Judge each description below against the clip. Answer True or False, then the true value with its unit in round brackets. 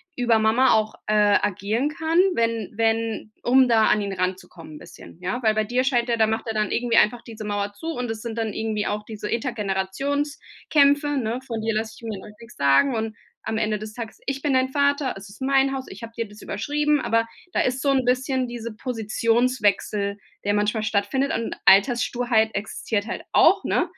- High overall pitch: True (225 Hz)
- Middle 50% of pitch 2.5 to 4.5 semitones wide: True (3.3 semitones)